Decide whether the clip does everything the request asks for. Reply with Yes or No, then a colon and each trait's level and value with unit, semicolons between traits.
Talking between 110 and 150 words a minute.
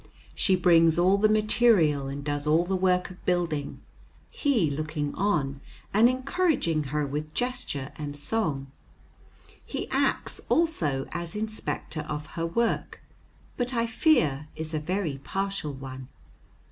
Yes: slow, 135 wpm